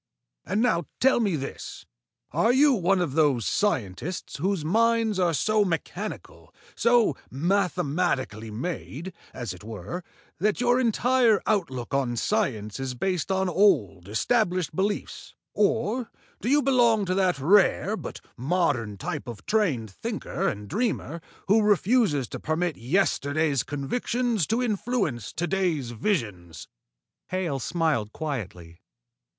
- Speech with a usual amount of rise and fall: No, wide, 8.2 semitones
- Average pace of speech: No, slow, 130 wpm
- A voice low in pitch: No, medium, 175 Hz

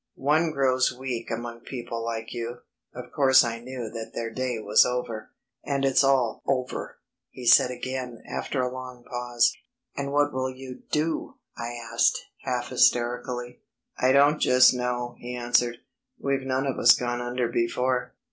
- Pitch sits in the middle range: No, low, 125 Hz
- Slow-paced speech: No, average, 160 wpm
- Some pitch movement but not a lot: No, narrow, 1.6 semitones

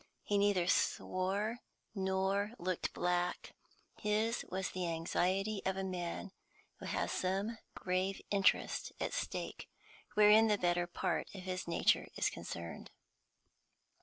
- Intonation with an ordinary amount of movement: No, narrow, 2.3 semitones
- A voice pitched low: No, high, 190 Hz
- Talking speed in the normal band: No, slow, 125 wpm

